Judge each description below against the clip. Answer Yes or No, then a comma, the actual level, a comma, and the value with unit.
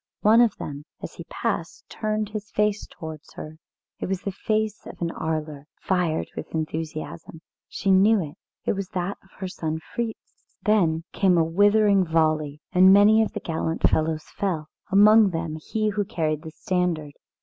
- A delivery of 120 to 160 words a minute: No, average, 170 wpm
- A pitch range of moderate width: Yes, average, 4.5 semitones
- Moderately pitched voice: Yes, medium, 180 Hz